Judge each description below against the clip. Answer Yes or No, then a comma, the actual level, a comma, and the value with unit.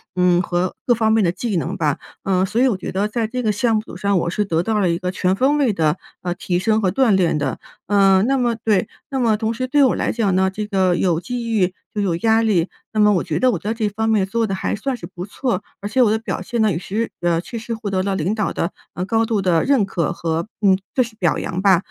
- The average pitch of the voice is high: Yes, high, 205 Hz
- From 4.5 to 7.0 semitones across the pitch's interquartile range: No, average, 3.7 semitones